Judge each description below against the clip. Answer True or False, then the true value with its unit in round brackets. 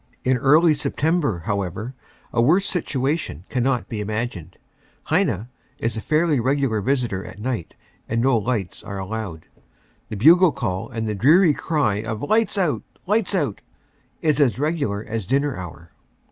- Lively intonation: True (6.1 semitones)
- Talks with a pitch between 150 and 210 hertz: False (125 Hz)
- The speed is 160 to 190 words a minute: False (150 wpm)